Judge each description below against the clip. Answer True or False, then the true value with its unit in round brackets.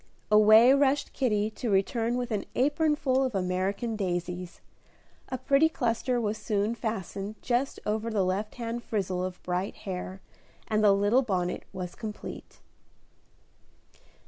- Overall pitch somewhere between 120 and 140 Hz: False (215 Hz)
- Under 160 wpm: True (140 wpm)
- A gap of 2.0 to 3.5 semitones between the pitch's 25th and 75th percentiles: False (4.1 semitones)